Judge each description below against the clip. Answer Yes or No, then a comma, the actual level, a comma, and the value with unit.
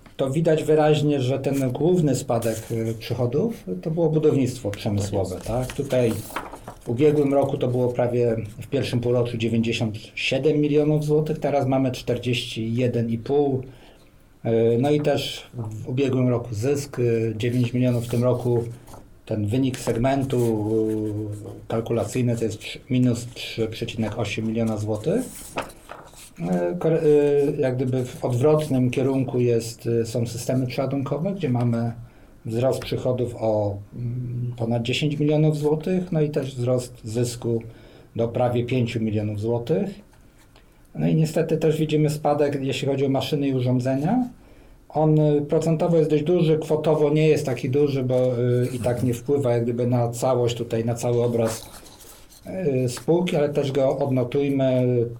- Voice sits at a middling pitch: No, low, 125 Hz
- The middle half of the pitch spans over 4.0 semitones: No, average, 3.7 semitones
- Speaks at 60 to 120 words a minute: No, average, 130 wpm